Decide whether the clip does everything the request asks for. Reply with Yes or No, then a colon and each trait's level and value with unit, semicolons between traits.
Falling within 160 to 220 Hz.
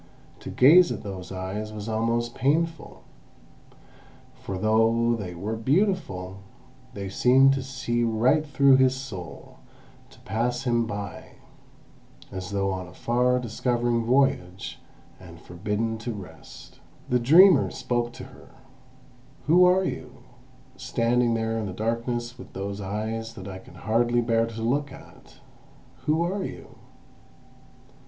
No: low, 115 Hz